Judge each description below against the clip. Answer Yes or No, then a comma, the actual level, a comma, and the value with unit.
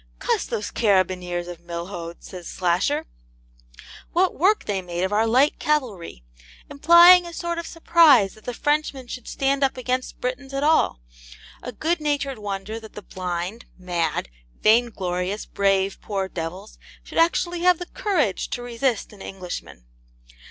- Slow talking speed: No, average, 150 wpm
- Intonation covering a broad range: Yes, wide, 7.8 semitones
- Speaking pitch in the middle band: No, high, 220 Hz